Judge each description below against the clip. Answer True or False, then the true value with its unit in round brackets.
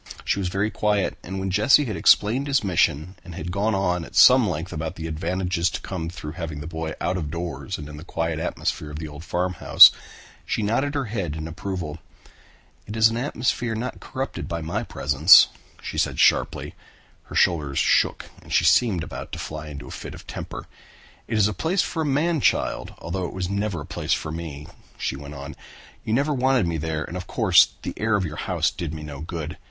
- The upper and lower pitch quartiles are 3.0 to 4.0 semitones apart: False (5.1 semitones)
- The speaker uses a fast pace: True (215 wpm)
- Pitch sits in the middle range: False (90 Hz)